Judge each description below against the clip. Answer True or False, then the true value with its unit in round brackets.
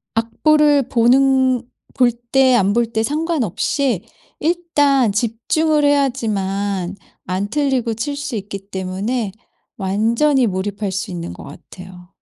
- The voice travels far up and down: True (5.8 semitones)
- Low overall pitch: False (230 Hz)